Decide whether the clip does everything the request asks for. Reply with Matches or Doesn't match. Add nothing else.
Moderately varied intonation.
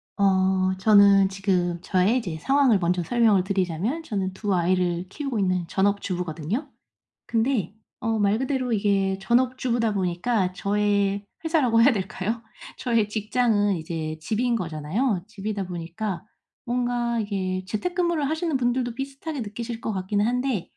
Matches